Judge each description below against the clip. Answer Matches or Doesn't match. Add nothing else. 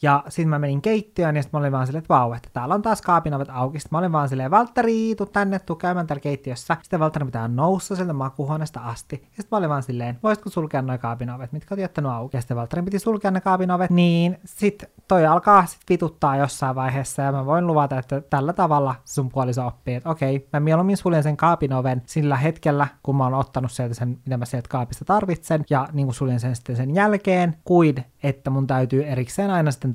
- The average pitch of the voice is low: Doesn't match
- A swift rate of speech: Matches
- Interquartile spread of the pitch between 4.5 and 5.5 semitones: Matches